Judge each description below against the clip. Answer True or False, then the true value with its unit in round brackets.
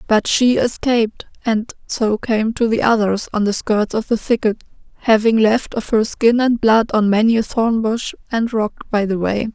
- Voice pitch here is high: True (220 Hz)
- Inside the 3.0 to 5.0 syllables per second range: True (4.5 syllables/s)